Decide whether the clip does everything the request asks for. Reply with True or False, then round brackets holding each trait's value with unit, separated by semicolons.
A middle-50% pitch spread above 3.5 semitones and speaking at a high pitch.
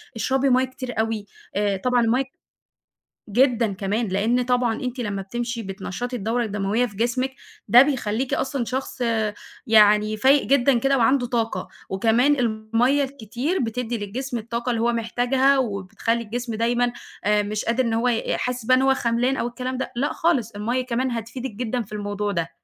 False (2.9 semitones; 235 Hz)